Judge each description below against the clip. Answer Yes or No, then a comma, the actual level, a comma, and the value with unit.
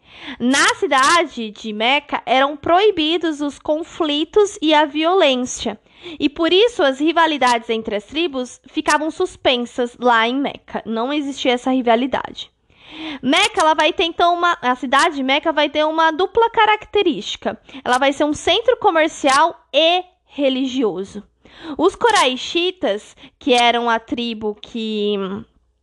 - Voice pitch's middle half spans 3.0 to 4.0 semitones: No, average, 5.3 semitones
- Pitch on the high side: Yes, very high, 295 Hz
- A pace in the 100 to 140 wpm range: Yes, average, 135 wpm